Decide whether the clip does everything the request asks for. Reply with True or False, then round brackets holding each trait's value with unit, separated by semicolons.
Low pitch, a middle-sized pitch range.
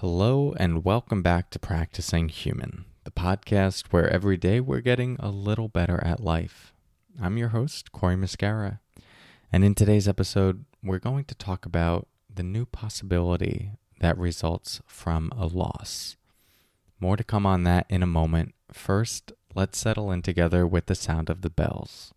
True (95 Hz; 3.6 semitones)